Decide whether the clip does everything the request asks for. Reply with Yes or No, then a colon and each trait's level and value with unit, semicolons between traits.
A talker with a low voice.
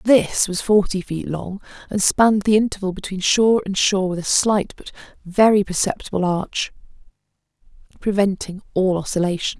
No: high, 195 Hz